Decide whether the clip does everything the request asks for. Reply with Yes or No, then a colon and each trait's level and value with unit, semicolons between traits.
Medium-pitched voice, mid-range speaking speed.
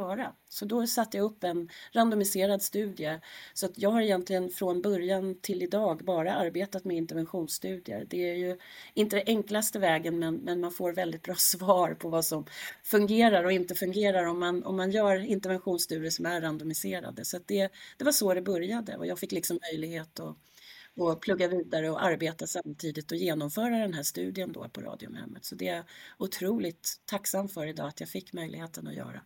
Yes: medium, 180 Hz; average, 185 wpm